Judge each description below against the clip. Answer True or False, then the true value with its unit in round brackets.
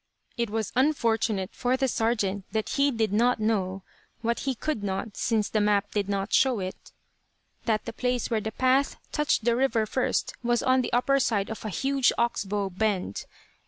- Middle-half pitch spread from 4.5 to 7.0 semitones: False (3.3 semitones)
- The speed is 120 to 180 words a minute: False (190 wpm)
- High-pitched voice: True (225 Hz)